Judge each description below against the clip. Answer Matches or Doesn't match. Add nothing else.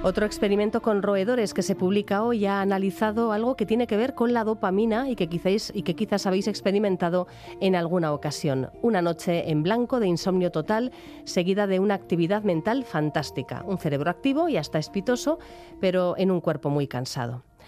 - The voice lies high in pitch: Matches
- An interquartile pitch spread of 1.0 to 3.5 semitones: Doesn't match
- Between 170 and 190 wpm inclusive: Matches